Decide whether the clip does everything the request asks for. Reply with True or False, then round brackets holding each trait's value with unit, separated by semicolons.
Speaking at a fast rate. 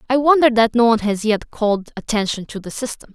True (230 wpm)